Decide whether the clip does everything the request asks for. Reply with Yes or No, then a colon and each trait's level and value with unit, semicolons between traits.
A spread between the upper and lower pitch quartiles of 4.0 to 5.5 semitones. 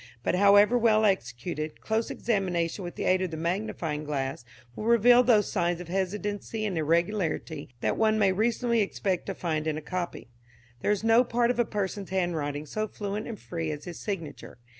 Yes: average, 4.6 semitones